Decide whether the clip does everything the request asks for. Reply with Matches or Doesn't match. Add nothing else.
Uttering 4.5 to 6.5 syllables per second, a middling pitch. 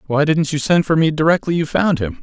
Matches